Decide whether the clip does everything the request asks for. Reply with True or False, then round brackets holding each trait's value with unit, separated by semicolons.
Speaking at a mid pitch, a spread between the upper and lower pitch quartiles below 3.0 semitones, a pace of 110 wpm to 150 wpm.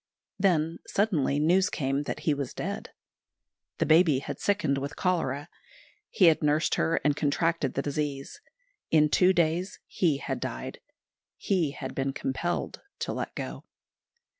False (155 Hz; 3.6 semitones; 145 wpm)